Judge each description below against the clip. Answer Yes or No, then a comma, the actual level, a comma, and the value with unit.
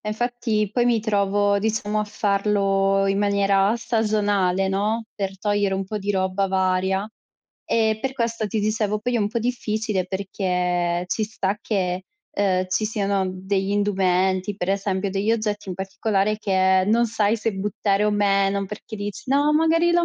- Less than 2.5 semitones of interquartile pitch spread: Yes, narrow, 2.0 semitones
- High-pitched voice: Yes, high, 205 Hz